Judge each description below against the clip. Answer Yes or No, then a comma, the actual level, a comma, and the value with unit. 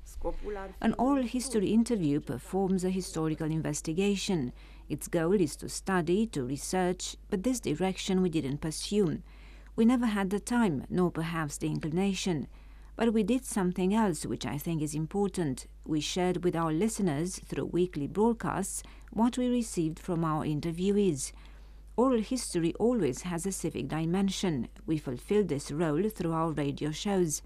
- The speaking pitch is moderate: Yes, medium, 180 Hz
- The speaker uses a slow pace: No, average, 150 wpm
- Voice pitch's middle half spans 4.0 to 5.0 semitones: Yes, average, 4.5 semitones